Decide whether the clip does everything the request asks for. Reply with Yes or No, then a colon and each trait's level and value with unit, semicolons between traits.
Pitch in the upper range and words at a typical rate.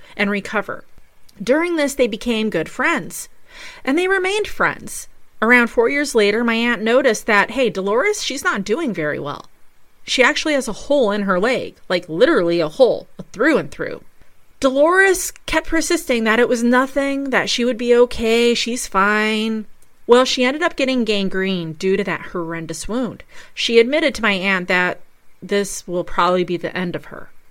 Yes: high, 235 Hz; average, 175 wpm